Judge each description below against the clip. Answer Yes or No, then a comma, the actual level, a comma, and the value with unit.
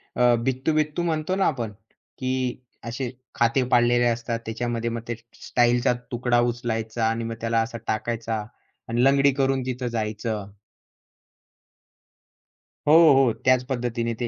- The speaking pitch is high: No, low, 120 Hz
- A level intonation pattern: Yes, narrow, 1.9 semitones